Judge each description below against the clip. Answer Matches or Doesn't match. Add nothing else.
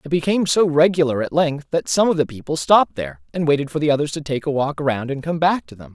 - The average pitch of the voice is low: Doesn't match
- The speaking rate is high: Matches